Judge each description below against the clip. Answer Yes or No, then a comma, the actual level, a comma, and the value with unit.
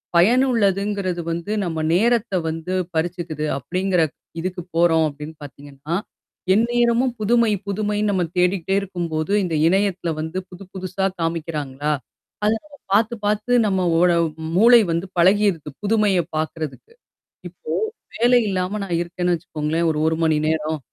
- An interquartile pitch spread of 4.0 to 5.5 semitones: Yes, average, 4.3 semitones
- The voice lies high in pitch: No, medium, 180 Hz